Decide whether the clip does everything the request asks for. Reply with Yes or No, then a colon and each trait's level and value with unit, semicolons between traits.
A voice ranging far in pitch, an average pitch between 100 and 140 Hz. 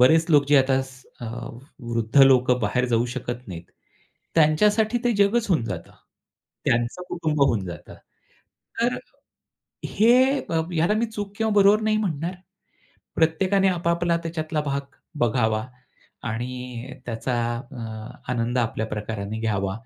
Yes: wide, 7.0 semitones; low, 135 Hz